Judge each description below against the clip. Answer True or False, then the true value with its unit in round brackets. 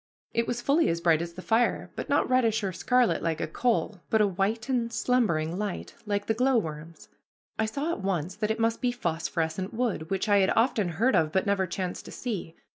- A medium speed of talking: False (215 wpm)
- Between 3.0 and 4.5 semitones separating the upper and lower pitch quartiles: False (5.2 semitones)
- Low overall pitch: False (205 Hz)